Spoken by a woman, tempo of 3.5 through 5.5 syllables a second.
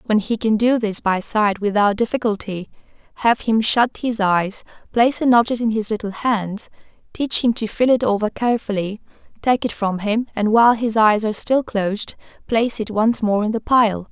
Yes: female; 5.1 syllables/s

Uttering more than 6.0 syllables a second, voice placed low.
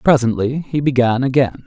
No: 5.1 syllables/s; low, 130 Hz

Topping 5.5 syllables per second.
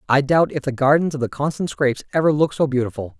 Yes: 7.0 syllables/s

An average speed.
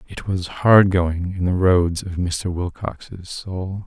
Yes: average, 170 wpm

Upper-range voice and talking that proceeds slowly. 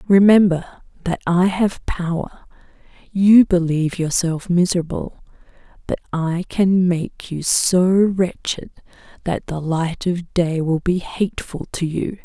No: medium, 175 Hz; slow, 125 wpm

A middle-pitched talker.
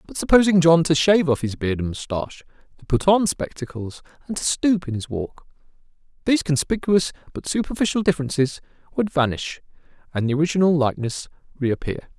Yes: medium, 155 Hz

